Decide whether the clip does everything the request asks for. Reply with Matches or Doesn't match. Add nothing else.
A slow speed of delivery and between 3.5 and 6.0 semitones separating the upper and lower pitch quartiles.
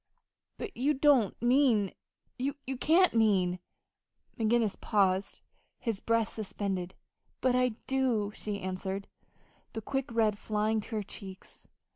Matches